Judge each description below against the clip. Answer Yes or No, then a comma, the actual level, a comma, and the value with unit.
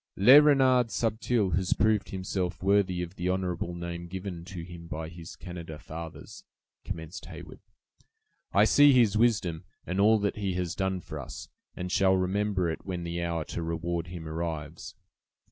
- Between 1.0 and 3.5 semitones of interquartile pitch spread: Yes, average, 3.0 semitones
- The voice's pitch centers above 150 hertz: No, very low, 90 Hz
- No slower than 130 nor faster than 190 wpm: Yes, average, 165 wpm